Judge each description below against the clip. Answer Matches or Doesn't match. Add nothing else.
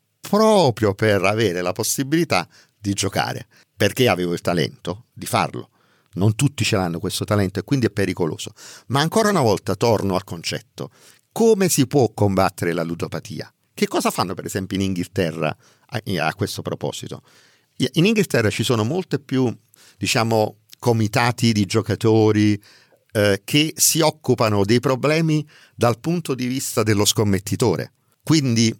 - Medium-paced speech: Matches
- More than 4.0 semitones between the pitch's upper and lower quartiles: Matches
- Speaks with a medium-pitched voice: Doesn't match